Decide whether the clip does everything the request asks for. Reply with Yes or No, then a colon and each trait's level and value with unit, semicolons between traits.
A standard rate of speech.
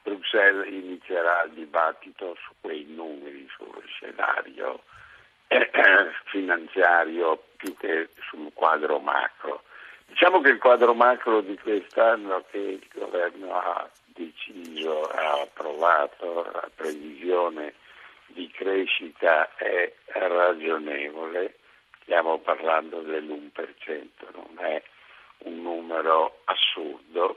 No: slow, 95 wpm